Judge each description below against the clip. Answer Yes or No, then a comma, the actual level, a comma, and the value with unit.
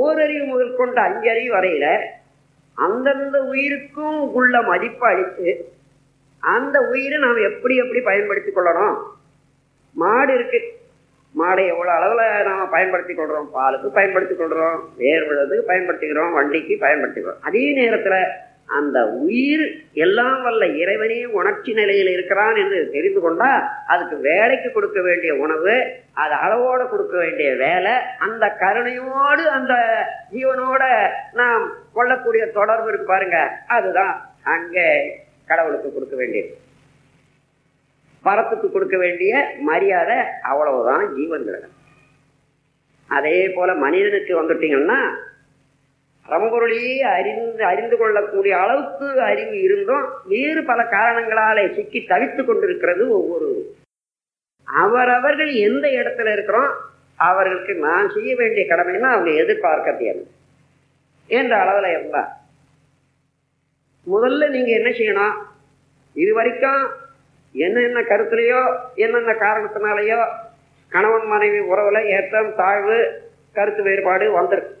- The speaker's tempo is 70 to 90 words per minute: No, average, 105 wpm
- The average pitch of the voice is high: Yes, high, 235 Hz